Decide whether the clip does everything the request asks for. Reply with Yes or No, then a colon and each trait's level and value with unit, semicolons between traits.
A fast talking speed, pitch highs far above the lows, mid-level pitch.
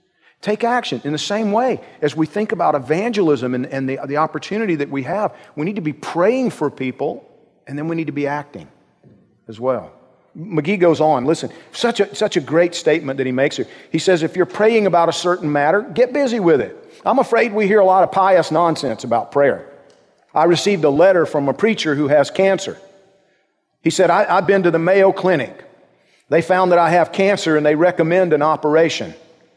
No: fast, 210 wpm; average, 4.7 semitones; medium, 170 Hz